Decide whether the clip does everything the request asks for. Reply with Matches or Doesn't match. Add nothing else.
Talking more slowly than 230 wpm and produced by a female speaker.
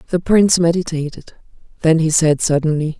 Matches